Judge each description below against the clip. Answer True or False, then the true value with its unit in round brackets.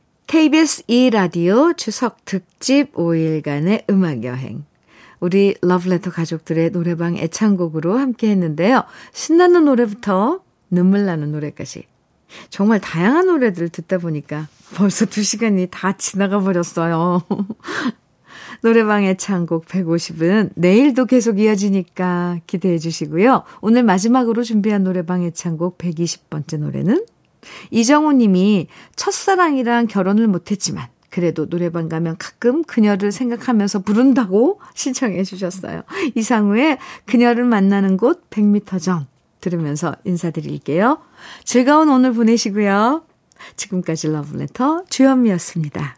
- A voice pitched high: True (200 Hz)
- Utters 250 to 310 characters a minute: True (290 characters per minute)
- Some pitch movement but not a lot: False (5.8 semitones)